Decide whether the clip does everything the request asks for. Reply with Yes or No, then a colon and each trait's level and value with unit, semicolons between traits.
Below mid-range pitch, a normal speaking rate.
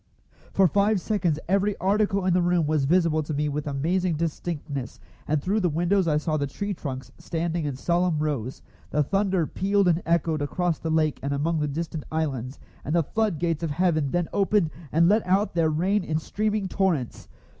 No: medium, 165 Hz; average, 195 wpm